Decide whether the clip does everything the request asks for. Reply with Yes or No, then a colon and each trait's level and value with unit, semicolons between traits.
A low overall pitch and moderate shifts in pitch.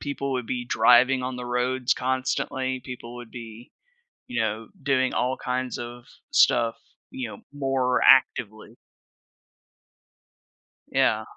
No: low, 125 Hz; narrow, 1.4 semitones